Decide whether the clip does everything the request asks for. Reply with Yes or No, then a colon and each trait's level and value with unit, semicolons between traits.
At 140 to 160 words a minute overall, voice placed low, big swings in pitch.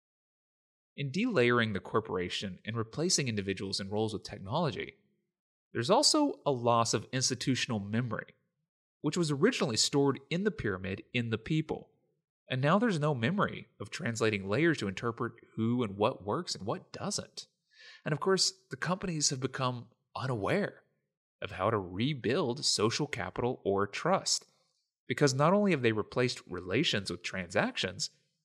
Yes: average, 150 wpm; low, 130 Hz; wide, 6.3 semitones